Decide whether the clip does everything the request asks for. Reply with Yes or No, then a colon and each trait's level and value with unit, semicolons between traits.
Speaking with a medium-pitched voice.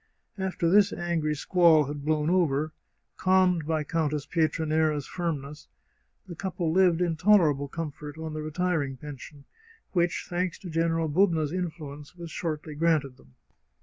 Yes: medium, 160 Hz